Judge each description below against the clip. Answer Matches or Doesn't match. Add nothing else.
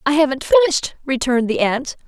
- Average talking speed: Matches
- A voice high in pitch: Matches